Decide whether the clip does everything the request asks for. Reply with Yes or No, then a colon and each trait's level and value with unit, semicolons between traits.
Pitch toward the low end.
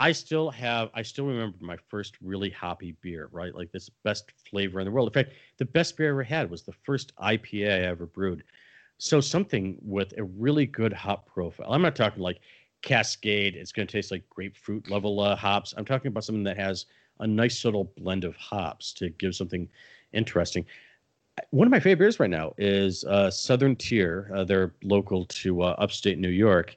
Yes: low, 100 Hz